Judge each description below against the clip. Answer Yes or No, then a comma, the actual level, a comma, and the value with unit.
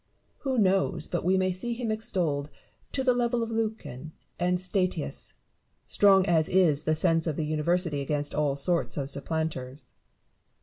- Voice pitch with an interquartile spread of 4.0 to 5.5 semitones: Yes, average, 4.4 semitones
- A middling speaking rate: Yes, average, 160 wpm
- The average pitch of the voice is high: No, medium, 175 Hz